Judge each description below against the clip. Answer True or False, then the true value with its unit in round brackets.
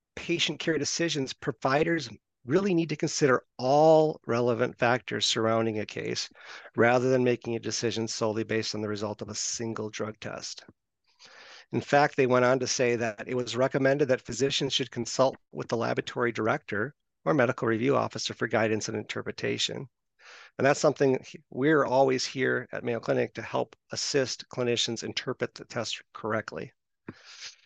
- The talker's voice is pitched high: False (125 Hz)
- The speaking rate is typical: True (160 wpm)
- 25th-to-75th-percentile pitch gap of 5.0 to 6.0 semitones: False (4.1 semitones)